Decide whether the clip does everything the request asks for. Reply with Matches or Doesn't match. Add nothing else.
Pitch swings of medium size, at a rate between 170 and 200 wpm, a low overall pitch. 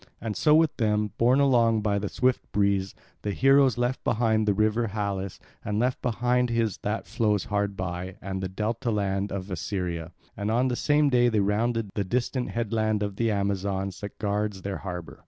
Matches